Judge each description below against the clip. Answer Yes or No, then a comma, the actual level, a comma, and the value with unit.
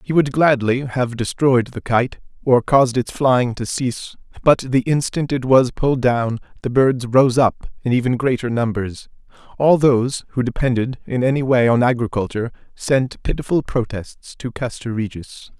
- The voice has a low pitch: Yes, low, 125 Hz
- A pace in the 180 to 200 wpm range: No, average, 165 wpm